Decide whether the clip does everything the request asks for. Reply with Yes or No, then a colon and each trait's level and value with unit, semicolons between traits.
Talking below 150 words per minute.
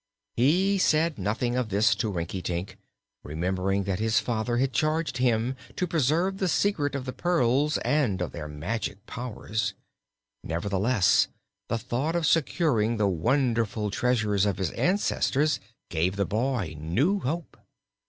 Yes: average, 140 wpm